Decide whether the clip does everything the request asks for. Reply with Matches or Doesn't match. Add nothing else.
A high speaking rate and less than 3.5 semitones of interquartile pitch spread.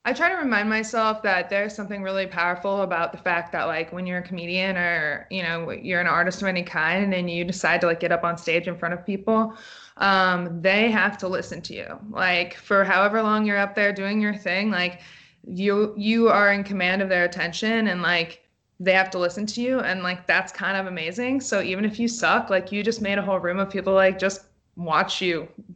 Matches